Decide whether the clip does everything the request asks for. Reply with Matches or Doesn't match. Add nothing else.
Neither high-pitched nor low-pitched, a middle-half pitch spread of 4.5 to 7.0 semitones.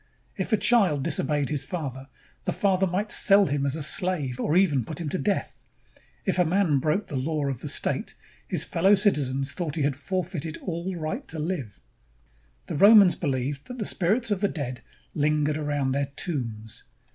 Matches